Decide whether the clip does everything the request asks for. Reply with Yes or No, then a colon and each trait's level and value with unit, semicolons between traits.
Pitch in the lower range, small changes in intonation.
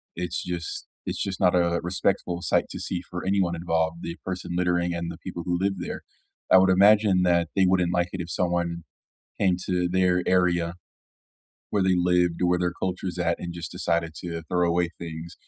Yes: very low, 90 Hz; narrow, 1.2 semitones